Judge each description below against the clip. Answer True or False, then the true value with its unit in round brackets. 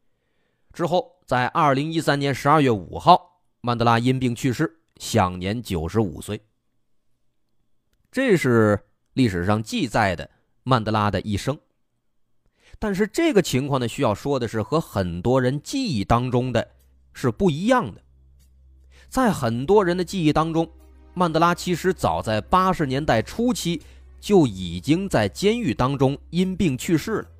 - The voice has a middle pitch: False (130 Hz)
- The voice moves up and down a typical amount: False (8.2 semitones)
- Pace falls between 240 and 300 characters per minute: False (220 characters per minute)